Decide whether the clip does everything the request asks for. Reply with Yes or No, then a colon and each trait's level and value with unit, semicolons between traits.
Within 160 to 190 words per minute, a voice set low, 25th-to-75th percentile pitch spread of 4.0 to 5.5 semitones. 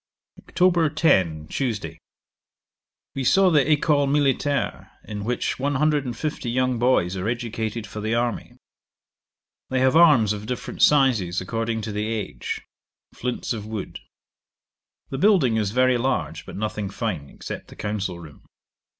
No: average, 145 wpm; low, 120 Hz; average, 4.7 semitones